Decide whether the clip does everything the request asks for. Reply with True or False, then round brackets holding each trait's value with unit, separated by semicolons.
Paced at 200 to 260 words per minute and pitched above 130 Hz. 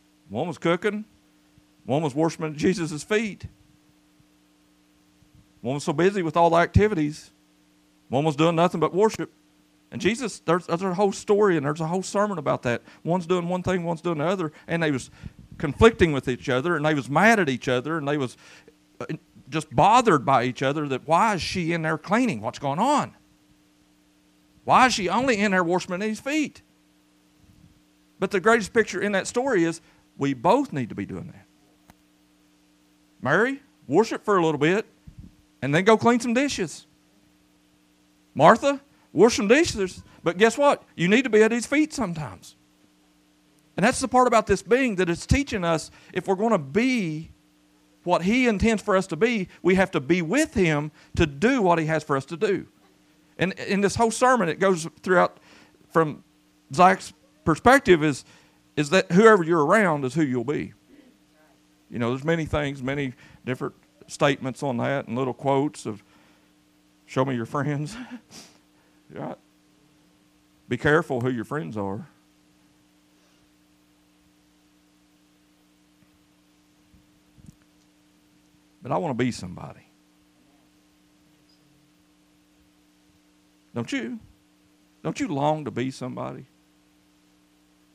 False (155 wpm; 140 Hz)